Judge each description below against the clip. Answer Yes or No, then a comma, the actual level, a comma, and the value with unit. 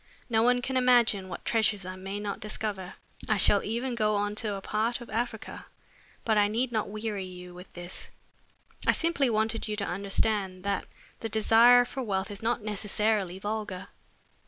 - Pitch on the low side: No, high, 215 Hz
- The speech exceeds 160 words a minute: Yes, average, 180 wpm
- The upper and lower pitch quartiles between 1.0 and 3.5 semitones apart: Yes, narrow, 2.6 semitones